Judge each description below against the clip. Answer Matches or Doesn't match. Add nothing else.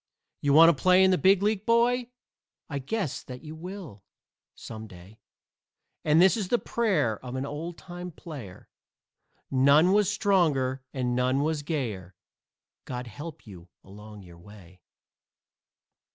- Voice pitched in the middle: Matches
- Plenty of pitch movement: Matches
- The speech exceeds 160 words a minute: Doesn't match